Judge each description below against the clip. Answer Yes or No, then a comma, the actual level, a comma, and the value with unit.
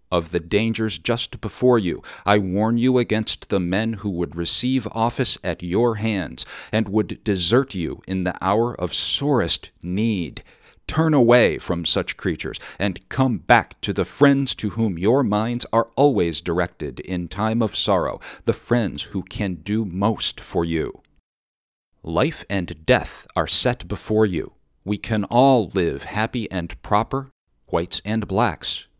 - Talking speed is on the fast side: No, average, 155 wpm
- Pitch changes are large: No, average, 4.3 semitones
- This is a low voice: Yes, low, 105 Hz